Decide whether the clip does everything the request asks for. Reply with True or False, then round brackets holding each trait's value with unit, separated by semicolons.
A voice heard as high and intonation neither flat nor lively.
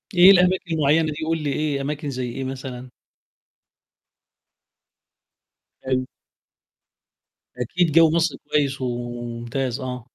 False (135 Hz; 3.9 semitones)